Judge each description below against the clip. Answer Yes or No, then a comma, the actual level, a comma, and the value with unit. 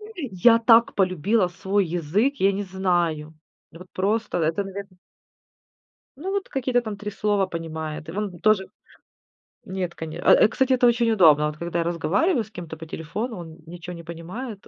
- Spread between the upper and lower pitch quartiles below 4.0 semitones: No, average, 4.5 semitones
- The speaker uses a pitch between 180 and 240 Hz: Yes, high, 190 Hz